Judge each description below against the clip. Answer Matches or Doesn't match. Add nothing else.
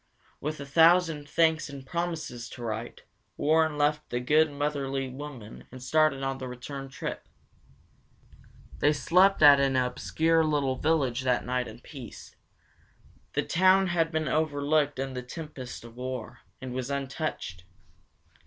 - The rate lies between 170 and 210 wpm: Doesn't match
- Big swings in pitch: Doesn't match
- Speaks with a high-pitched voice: Doesn't match